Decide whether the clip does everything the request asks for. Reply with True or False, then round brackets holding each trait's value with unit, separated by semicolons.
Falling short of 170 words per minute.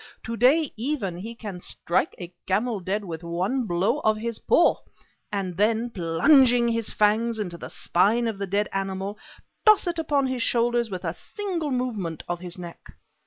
False (175 wpm)